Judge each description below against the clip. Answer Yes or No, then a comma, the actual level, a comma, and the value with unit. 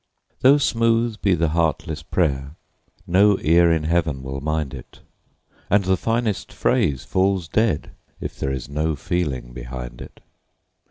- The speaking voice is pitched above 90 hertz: No, very low, 80 Hz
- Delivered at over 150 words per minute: No, average, 145 wpm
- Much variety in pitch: Yes, wide, 6.0 semitones